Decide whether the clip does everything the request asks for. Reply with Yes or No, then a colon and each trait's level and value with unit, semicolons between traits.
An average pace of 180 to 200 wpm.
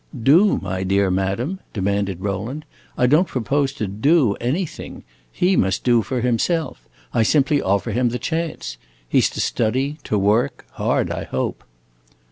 No: average, 155 wpm